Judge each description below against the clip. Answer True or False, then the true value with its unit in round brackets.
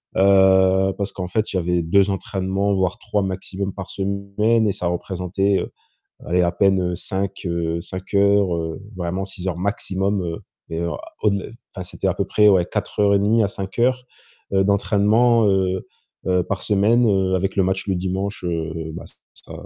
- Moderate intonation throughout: False (1.7 semitones)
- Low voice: True (95 Hz)